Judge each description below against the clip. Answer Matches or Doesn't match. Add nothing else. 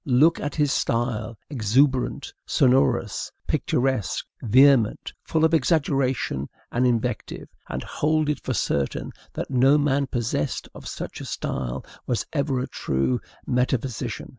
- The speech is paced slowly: Matches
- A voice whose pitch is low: Matches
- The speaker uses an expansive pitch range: Doesn't match